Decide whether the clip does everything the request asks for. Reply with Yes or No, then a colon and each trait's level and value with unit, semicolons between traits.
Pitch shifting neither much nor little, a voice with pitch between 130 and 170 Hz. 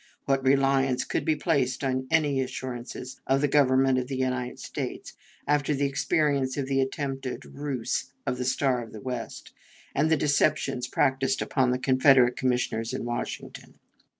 No: narrow, 1.6 semitones; low, 135 Hz